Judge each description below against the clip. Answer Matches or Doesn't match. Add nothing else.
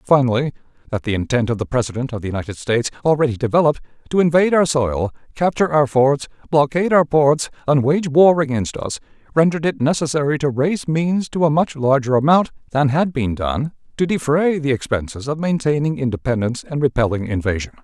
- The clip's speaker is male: Matches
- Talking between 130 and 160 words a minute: Doesn't match